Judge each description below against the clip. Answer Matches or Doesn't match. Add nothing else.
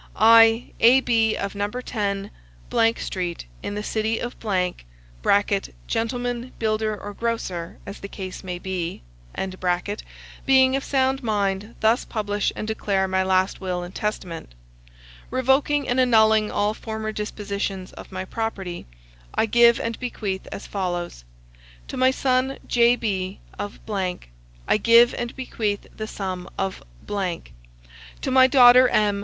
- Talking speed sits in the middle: Doesn't match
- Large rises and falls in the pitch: Doesn't match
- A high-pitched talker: Matches